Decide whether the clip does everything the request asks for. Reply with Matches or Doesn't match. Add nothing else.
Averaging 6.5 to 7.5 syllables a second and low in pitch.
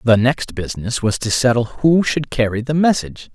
Doesn't match